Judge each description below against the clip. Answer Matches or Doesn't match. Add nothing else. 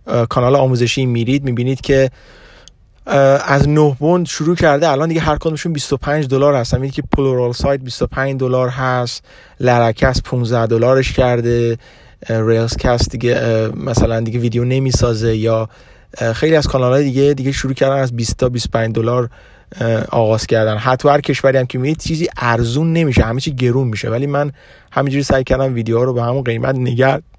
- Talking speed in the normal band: Doesn't match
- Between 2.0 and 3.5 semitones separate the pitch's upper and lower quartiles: Matches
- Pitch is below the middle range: Matches